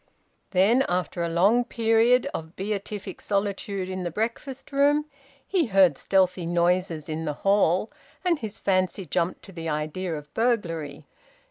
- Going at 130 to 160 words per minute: Yes, average, 145 wpm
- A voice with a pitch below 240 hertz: Yes, high, 190 Hz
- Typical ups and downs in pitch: Yes, average, 4.6 semitones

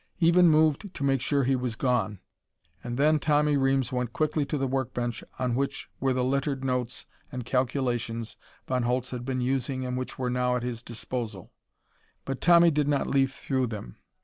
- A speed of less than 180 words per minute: No, average, 190 wpm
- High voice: No, low, 130 Hz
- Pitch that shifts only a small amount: Yes, narrow, 2.0 semitones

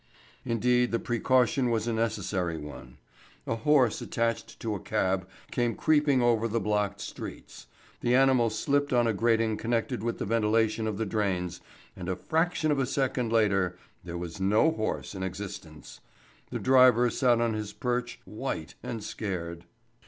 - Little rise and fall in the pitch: No, average, 3.8 semitones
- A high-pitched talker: No, low, 115 Hz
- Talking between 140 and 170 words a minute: Yes, average, 160 wpm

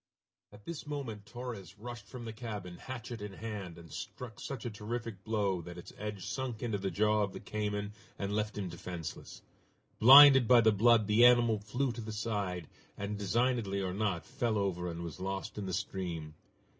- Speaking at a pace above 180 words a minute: Yes, average, 190 wpm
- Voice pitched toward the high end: No, low, 105 Hz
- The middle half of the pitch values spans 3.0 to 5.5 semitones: Yes, average, 3.4 semitones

